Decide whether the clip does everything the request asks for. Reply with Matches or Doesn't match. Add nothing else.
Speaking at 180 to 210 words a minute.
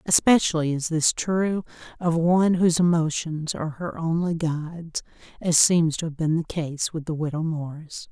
Doesn't match